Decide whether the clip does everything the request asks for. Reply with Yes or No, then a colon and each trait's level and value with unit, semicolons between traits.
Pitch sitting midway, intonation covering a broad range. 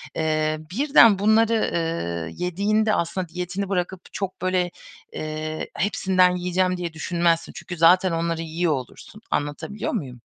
No: medium, 180 Hz; average, 2.9 semitones